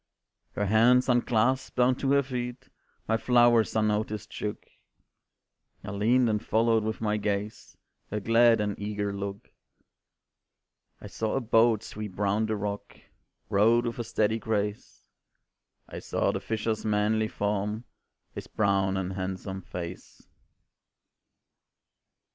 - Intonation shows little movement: Yes, narrow, 2.1 semitones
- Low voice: Yes, low, 110 Hz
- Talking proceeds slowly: Yes, slow, 125 wpm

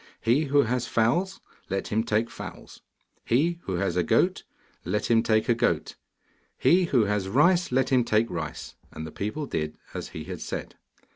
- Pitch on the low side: Yes, low, 115 Hz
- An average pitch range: No, wide, 5.9 semitones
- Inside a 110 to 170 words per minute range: No, average, 185 wpm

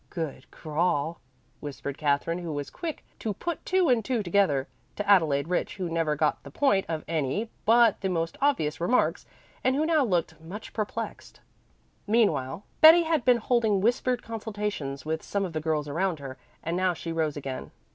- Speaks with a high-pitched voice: No, medium, 180 Hz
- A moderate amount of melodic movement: No, wide, 6.6 semitones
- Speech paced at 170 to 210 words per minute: Yes, average, 175 wpm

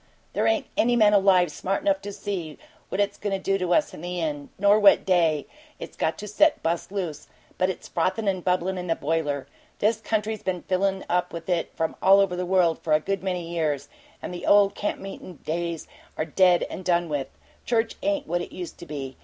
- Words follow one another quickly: Yes, fast, 220 wpm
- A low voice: No, medium, 180 Hz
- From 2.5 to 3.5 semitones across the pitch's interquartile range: Yes, average, 3.1 semitones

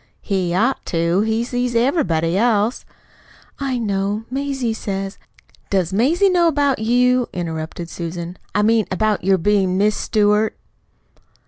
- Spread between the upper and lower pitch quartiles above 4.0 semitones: Yes, average, 4.7 semitones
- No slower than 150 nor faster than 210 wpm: No, slow, 135 wpm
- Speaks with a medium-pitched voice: No, high, 210 Hz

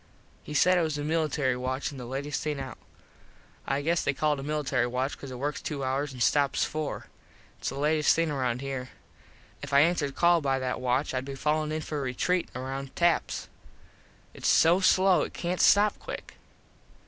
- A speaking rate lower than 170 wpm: No, average, 195 wpm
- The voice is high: No, medium, 145 Hz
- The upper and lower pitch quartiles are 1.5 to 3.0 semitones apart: Yes, average, 2.7 semitones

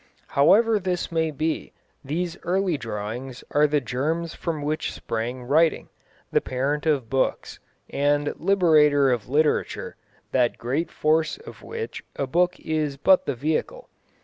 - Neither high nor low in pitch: Yes, medium, 150 Hz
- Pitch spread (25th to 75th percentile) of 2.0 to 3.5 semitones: No, average, 3.9 semitones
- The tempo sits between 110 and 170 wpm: Yes, average, 140 wpm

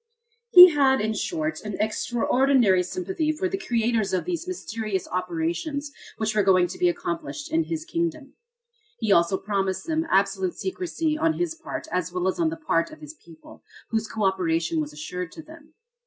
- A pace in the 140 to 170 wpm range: No, average, 180 wpm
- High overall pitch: Yes, high, 230 Hz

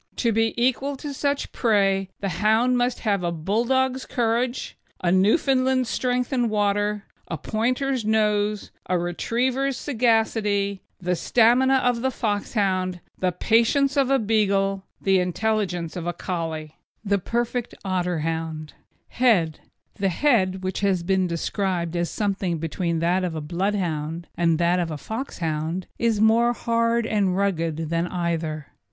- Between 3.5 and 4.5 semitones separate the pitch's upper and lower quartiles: No, average, 5.1 semitones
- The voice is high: Yes, high, 200 Hz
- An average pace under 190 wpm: Yes, average, 140 wpm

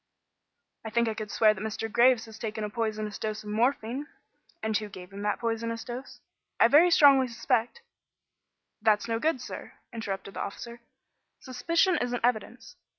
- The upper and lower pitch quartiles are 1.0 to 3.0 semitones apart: Yes, narrow, 2.4 semitones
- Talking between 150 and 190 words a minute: Yes, average, 170 wpm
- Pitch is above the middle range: Yes, high, 230 Hz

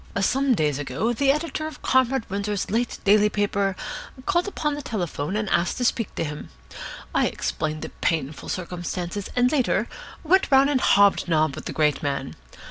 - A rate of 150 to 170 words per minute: No, average, 180 wpm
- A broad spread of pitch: Yes, wide, 8.2 semitones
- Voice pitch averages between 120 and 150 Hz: No, high, 205 Hz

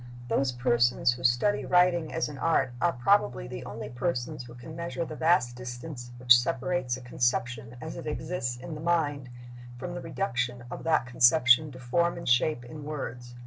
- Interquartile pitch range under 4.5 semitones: No, average, 4.8 semitones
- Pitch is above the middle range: No, low, 130 Hz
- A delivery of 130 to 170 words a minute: No, average, 185 wpm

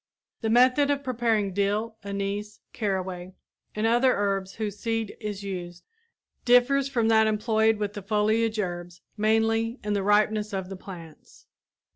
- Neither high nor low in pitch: No, high, 210 Hz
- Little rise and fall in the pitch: Yes, narrow, 2.3 semitones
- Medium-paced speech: Yes, average, 145 wpm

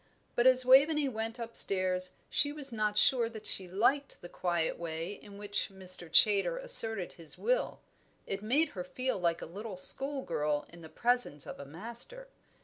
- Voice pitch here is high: Yes, high, 210 Hz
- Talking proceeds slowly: No, average, 175 wpm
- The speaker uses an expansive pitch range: Yes, wide, 6.2 semitones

